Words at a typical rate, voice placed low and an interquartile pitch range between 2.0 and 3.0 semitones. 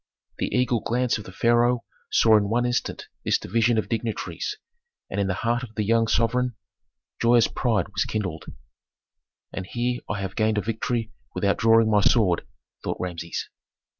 Yes: average, 165 wpm; low, 115 Hz; narrow, 2.6 semitones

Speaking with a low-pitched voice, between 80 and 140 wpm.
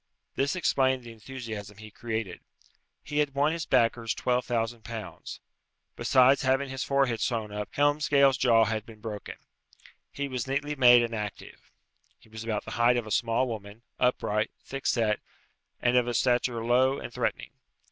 No: low, 120 Hz; average, 165 wpm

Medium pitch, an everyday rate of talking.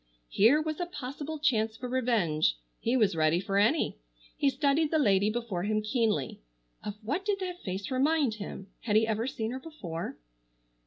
No: high, 230 Hz; average, 175 wpm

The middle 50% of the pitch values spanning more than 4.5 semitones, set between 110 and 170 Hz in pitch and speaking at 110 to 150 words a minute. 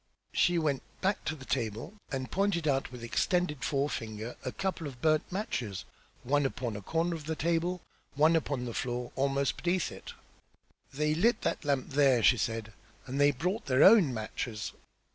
No: average, 5.2 semitones; medium, 140 Hz; average, 175 wpm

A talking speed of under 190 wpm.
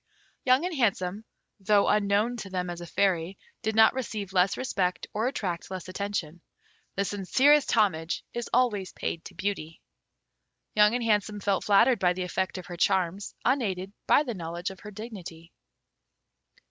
Yes: average, 160 wpm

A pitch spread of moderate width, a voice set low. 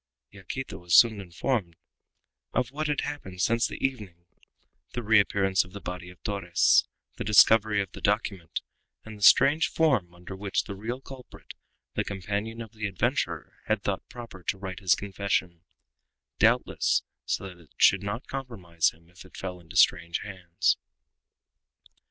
Yes: average, 3.8 semitones; low, 100 Hz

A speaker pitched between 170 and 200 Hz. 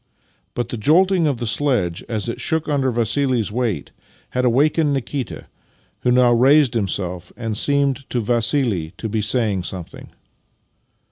No: low, 120 Hz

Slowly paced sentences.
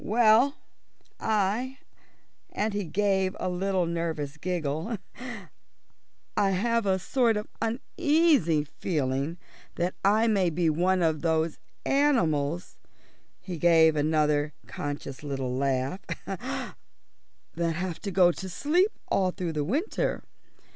Yes: slow, 115 wpm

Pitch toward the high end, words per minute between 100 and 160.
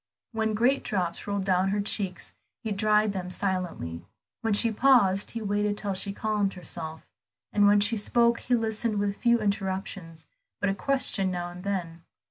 No: high, 205 Hz; average, 170 wpm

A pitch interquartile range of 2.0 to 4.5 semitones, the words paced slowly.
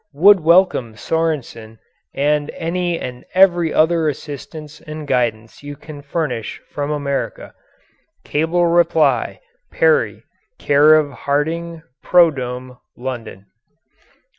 Yes: average, 4.1 semitones; slow, 100 wpm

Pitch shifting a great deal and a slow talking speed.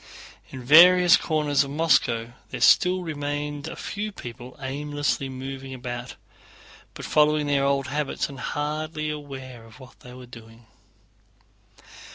No: average, 2.9 semitones; slow, 130 wpm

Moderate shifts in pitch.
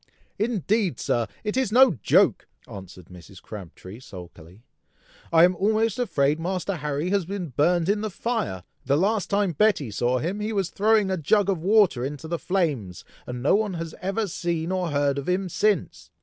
No: wide, 6.7 semitones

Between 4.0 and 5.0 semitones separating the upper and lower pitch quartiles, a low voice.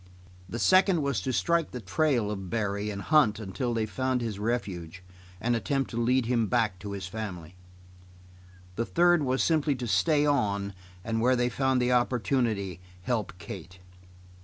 Yes: average, 4.6 semitones; low, 115 Hz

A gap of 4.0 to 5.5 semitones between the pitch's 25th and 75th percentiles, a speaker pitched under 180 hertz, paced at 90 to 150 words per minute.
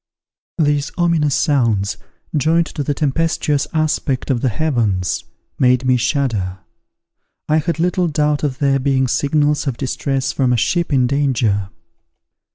No: average, 3.3 semitones; medium, 140 Hz; average, 140 wpm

